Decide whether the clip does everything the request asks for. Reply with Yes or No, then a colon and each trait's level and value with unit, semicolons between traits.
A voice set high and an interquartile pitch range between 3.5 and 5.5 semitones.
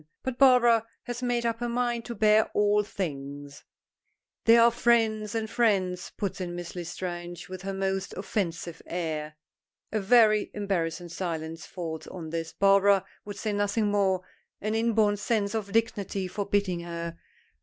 Yes: high, 200 Hz; average, 4.1 semitones